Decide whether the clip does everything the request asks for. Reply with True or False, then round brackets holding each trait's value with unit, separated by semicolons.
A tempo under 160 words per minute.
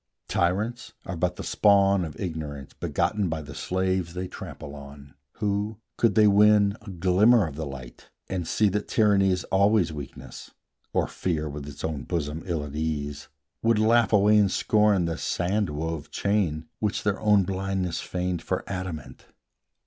False (165 wpm)